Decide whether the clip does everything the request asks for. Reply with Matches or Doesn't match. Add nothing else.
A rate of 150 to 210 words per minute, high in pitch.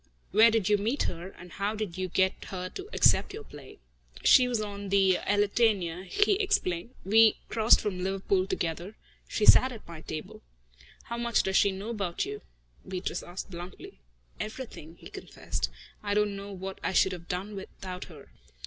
Matches